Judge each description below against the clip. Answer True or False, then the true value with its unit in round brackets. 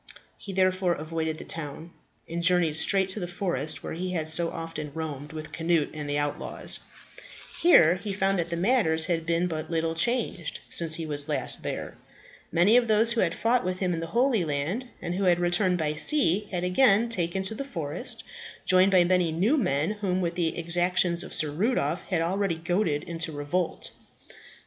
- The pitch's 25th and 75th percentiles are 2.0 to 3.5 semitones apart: True (3.0 semitones)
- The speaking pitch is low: False (175 Hz)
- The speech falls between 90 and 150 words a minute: False (185 wpm)